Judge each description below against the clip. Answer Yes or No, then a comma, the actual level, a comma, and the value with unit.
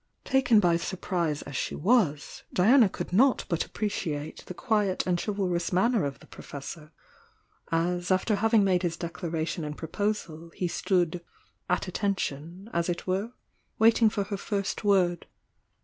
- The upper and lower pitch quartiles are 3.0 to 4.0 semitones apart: Yes, average, 3.6 semitones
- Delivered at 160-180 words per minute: No, average, 150 wpm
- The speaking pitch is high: No, medium, 180 Hz